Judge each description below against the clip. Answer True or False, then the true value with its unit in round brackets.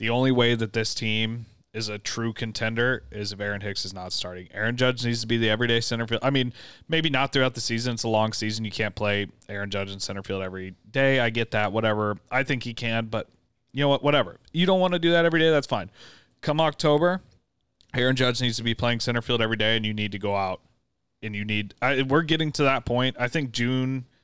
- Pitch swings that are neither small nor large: True (3.3 semitones)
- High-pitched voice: False (115 Hz)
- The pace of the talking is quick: True (250 wpm)